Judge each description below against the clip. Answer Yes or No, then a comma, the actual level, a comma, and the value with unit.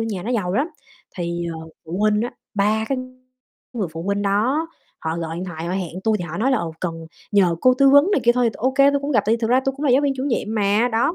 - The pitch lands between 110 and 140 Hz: No, high, 215 Hz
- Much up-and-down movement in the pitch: Yes, wide, 6.3 semitones